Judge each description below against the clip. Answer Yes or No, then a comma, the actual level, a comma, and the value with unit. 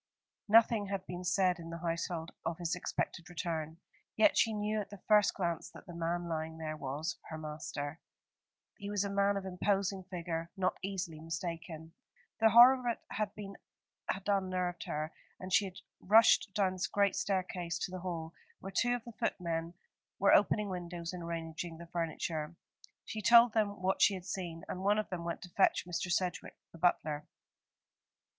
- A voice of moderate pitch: Yes, medium, 180 Hz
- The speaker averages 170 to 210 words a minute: Yes, average, 180 wpm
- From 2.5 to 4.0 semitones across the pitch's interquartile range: Yes, average, 3.1 semitones